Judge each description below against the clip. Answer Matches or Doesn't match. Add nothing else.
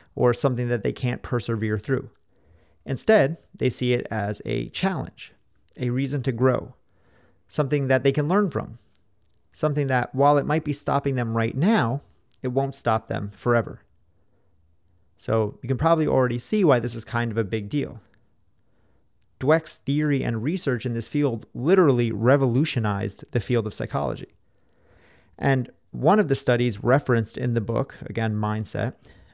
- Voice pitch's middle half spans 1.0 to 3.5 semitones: Doesn't match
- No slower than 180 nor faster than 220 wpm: Doesn't match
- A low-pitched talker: Matches